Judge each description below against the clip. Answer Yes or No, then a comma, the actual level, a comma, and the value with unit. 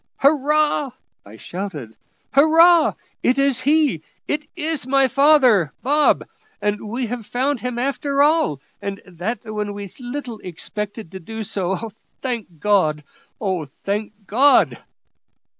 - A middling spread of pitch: No, wide, 6.0 semitones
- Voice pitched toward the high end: Yes, high, 235 Hz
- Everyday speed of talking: No, slow, 125 wpm